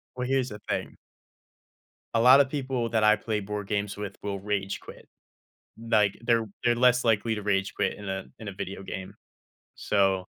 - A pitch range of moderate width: Yes, average, 3.0 semitones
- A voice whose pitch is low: Yes, low, 105 Hz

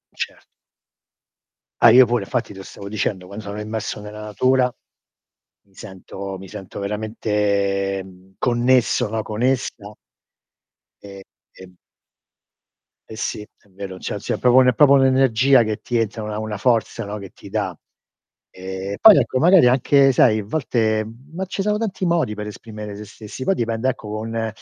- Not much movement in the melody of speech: No, average, 3.9 semitones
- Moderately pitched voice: No, low, 110 Hz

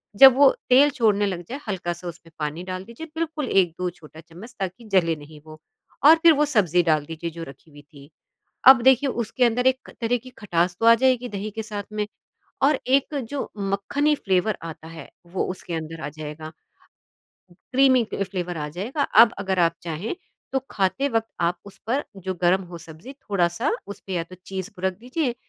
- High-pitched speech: Yes, high, 195 Hz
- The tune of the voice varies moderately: No, wide, 6.7 semitones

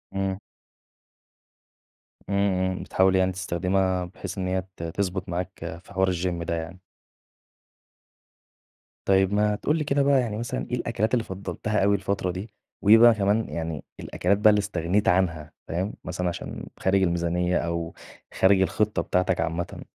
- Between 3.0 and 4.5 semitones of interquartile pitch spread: No, narrow, 2.6 semitones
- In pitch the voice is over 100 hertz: No, very low, 95 Hz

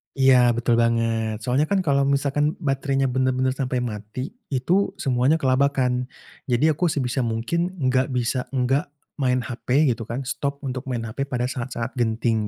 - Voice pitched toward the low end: Yes, low, 130 Hz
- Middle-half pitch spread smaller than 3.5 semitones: Yes, narrow, 2.5 semitones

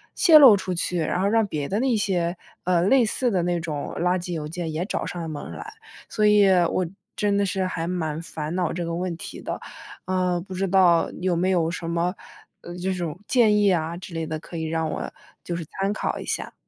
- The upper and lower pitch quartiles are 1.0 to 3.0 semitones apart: Yes, average, 2.7 semitones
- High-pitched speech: No, medium, 180 Hz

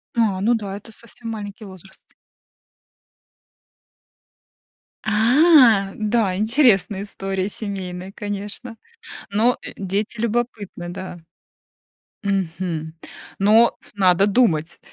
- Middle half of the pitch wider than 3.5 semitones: No, average, 3.0 semitones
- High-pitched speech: Yes, high, 205 Hz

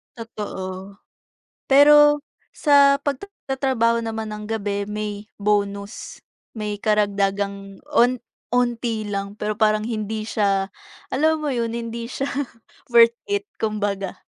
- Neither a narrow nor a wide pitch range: Yes, average, 3.3 semitones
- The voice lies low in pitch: No, high, 215 Hz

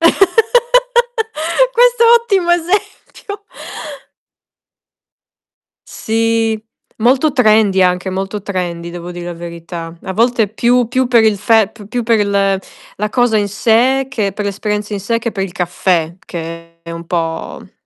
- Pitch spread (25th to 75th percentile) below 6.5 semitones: No, wide, 6.8 semitones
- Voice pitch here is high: Yes, high, 220 Hz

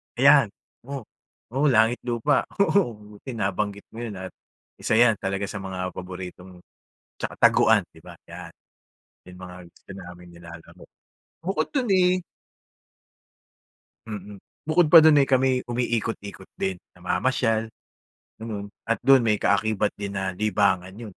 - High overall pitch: No, low, 105 Hz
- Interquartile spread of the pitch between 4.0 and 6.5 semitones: Yes, average, 4.5 semitones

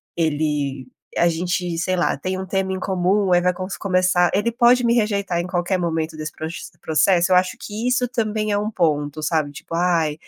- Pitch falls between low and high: Yes, medium, 180 Hz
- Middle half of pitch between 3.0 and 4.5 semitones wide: Yes, average, 3.5 semitones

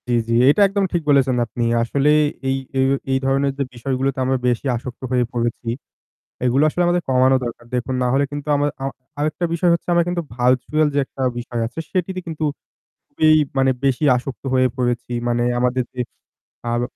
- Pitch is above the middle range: No, low, 135 Hz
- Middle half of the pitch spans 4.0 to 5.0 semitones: No, average, 3.3 semitones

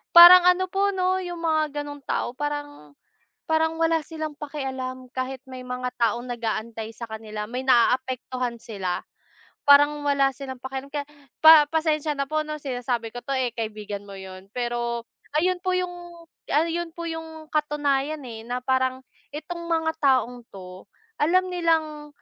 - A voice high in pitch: Yes, very high, 275 Hz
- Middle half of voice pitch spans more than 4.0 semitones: Yes, average, 4.6 semitones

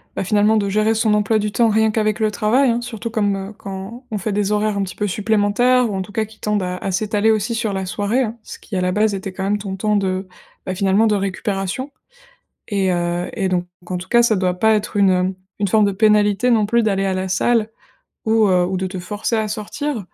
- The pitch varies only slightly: Yes, narrow, 2.3 semitones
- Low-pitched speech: No, high, 210 Hz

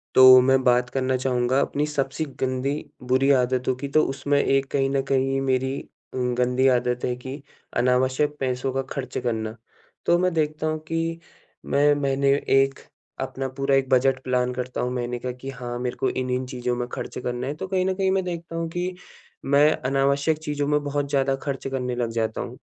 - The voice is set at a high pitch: No, low, 135 Hz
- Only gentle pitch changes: Yes, narrow, 2.2 semitones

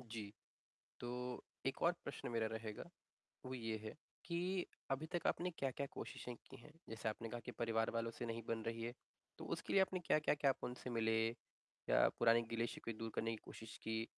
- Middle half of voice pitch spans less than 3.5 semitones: Yes, average, 3.1 semitones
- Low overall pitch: Yes, low, 115 Hz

